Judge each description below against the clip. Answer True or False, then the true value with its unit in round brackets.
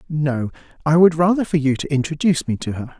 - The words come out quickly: True (220 wpm)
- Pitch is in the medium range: True (150 Hz)